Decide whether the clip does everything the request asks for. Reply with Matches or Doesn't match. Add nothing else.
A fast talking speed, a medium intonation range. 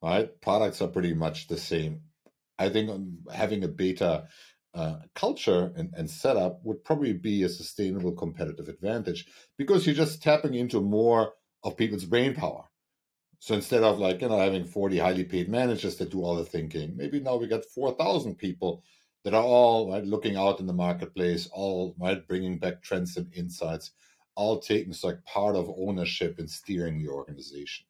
Doesn't match